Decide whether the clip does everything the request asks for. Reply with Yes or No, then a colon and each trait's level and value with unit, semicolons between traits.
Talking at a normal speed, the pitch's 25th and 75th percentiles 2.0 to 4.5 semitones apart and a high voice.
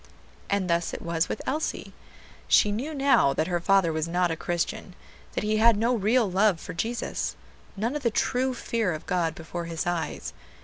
No: average, 190 wpm; wide, 5.5 semitones; high, 195 Hz